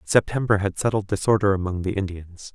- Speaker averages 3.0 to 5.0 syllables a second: No, 5.7 syllables/s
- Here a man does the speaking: Yes, male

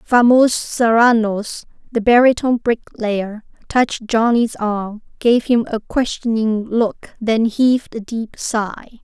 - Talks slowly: Yes, slow, 120 wpm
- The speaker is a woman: Yes, female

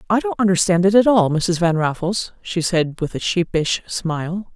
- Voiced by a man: No, female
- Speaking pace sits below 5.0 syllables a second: Yes, 4.8 syllables/s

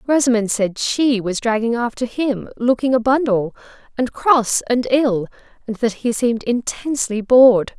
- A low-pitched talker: No, high, 235 Hz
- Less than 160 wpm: Yes, average, 140 wpm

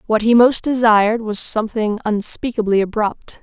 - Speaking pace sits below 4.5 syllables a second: No, 5.0 syllables/s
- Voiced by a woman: Yes, female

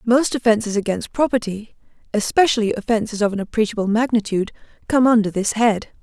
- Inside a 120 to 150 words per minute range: Yes, average, 140 wpm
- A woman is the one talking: Yes, female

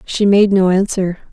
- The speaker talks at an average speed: Yes, average, 180 wpm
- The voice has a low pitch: No, high, 195 Hz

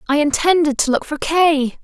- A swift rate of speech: No, average, 195 wpm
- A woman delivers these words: Yes, female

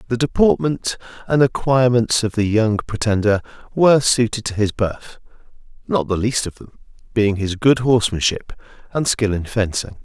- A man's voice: Yes, male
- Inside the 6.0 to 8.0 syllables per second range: No, 4.9 syllables/s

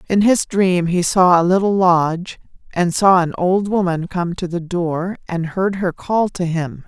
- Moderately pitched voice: Yes, medium, 180 Hz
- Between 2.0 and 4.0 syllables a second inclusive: No, 4.2 syllables/s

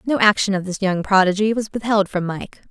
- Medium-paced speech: No, fast, 220 wpm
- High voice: Yes, high, 200 Hz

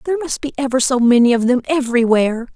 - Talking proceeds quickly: Yes, fast, 210 wpm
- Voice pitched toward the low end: No, very high, 255 Hz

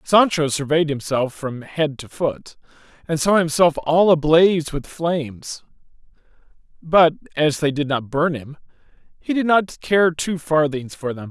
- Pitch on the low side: No, medium, 155 Hz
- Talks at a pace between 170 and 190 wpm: No, average, 155 wpm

